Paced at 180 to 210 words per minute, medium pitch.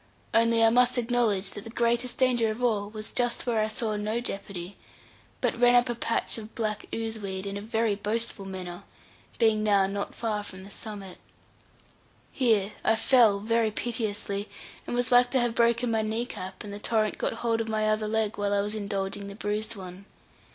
No: average, 200 wpm; high, 215 Hz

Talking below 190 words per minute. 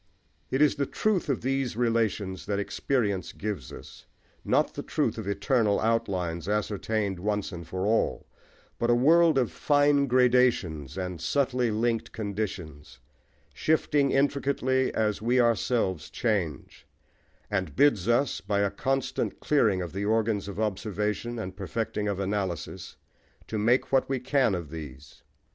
Yes: average, 140 wpm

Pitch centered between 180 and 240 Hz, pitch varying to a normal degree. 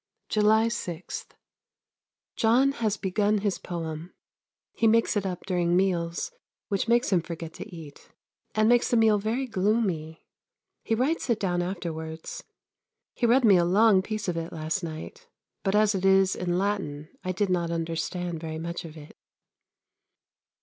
Yes: high, 190 Hz; average, 4.4 semitones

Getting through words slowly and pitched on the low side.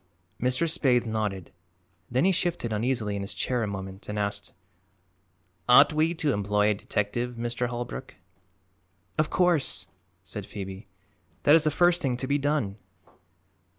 No: average, 150 wpm; low, 120 Hz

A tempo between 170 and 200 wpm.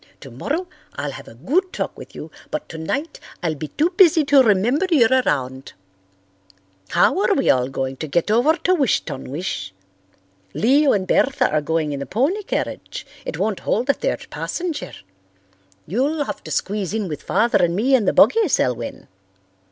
Yes: average, 175 wpm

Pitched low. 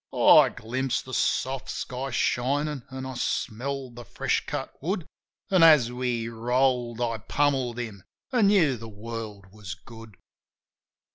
Yes: low, 125 Hz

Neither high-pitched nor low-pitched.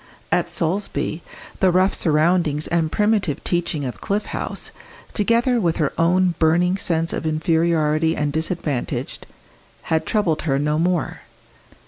Yes: medium, 165 Hz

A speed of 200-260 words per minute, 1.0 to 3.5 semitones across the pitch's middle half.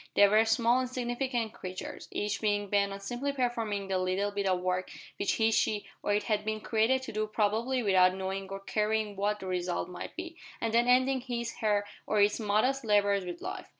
Yes: fast, 205 wpm; average, 3.0 semitones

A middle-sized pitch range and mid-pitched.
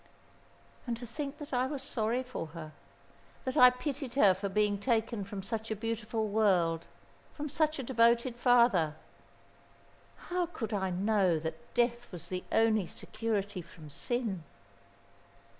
No: average, 4.5 semitones; high, 225 Hz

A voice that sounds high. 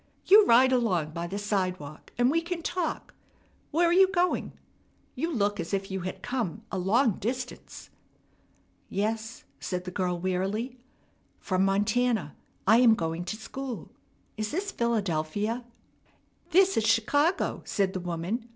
Yes: high, 220 Hz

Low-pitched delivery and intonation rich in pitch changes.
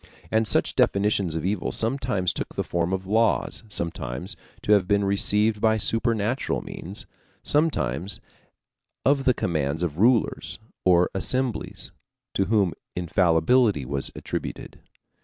No: low, 100 Hz; average, 4.4 semitones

